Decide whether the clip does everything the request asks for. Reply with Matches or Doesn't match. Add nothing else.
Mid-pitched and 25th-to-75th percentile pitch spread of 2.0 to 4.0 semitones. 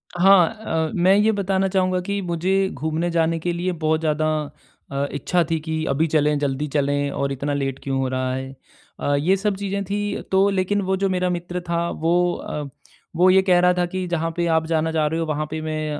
Matches